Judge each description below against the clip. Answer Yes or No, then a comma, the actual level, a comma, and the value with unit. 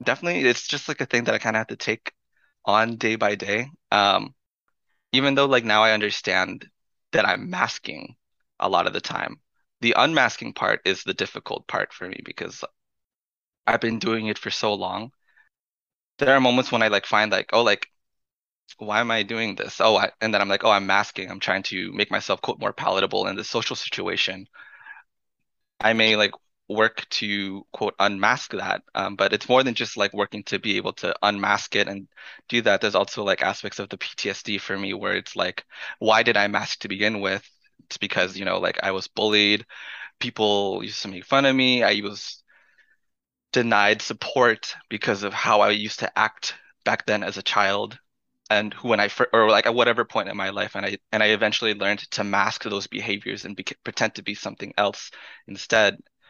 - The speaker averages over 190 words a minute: Yes, average, 200 wpm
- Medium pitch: No, low, 110 Hz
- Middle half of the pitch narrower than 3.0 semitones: Yes, narrow, 2.4 semitones